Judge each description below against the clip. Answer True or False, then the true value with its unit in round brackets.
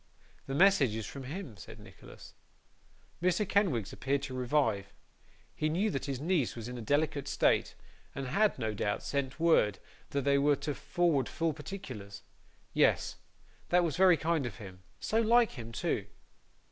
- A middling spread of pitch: False (5.9 semitones)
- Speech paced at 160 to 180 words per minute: True (165 wpm)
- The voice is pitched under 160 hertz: True (140 Hz)